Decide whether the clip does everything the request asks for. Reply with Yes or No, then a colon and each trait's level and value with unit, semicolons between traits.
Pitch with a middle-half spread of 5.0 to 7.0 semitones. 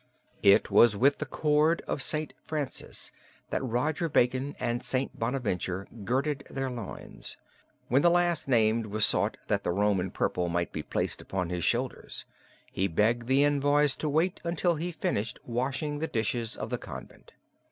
Yes: wide, 5.6 semitones